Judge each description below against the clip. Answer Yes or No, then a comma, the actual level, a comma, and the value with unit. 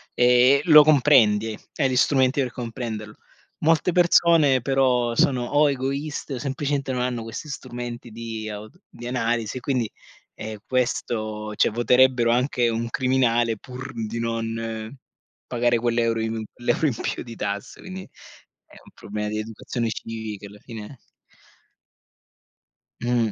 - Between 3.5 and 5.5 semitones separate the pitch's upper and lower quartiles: No, average, 2.7 semitones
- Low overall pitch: Yes, low, 120 Hz